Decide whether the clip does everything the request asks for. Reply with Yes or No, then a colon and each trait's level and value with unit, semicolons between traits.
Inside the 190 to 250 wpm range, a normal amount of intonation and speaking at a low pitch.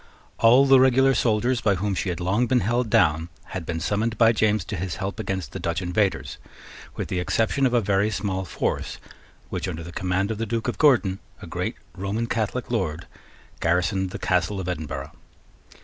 Yes: average, 195 wpm; average, 4.1 semitones; low, 100 Hz